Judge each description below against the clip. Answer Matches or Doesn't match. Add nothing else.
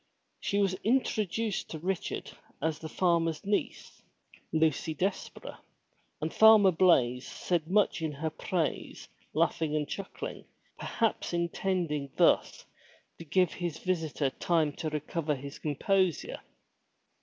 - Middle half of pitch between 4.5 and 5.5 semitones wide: Doesn't match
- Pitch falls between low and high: Matches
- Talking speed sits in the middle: Doesn't match